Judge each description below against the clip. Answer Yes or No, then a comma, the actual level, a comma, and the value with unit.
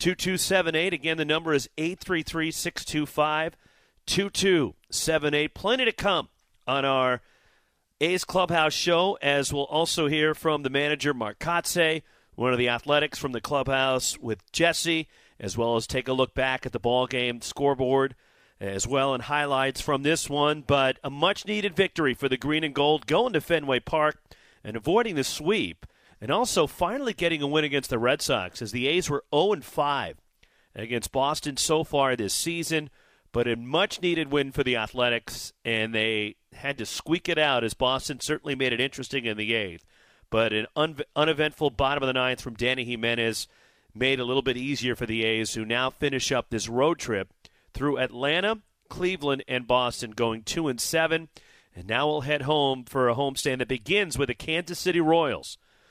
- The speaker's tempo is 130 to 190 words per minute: Yes, average, 180 wpm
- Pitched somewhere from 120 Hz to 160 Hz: Yes, medium, 140 Hz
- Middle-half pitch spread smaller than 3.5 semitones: No, average, 4.1 semitones